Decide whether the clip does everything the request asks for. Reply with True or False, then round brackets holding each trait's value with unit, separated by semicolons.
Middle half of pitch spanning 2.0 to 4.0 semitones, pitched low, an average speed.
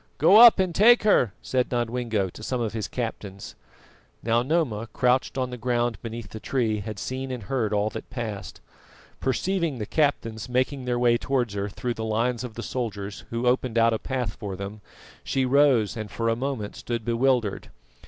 True (2.9 semitones; 120 Hz; 190 wpm)